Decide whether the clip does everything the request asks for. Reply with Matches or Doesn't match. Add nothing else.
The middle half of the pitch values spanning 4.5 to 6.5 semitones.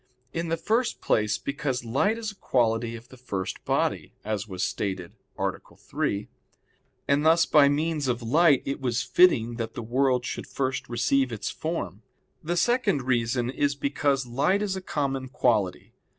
Matches